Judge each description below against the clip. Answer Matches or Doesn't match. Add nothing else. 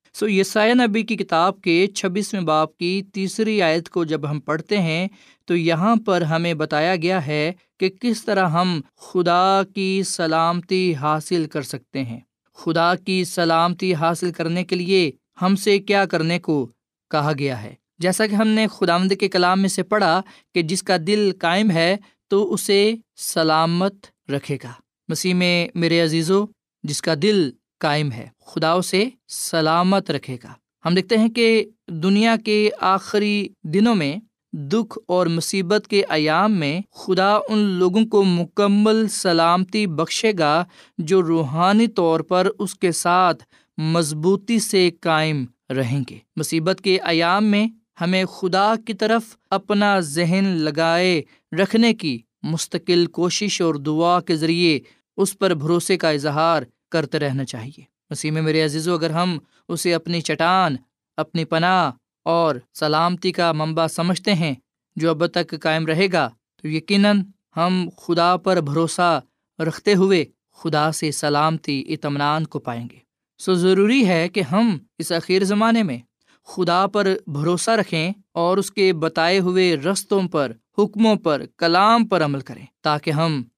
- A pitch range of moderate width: Matches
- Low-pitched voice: Doesn't match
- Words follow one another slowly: Doesn't match